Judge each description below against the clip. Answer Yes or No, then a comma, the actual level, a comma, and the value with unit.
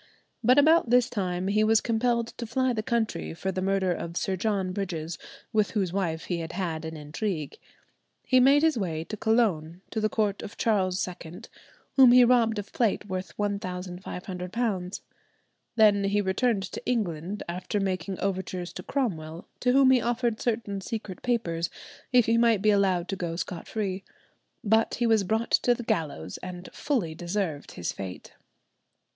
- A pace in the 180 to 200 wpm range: No, average, 170 wpm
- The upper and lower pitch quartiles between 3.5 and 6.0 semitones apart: Yes, average, 4.3 semitones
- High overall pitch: Yes, high, 200 Hz